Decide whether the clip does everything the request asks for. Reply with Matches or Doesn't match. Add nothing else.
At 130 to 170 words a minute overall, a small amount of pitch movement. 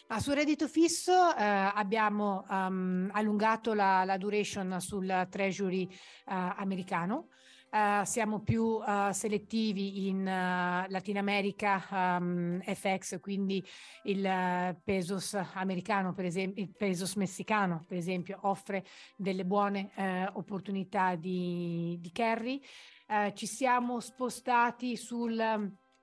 Doesn't match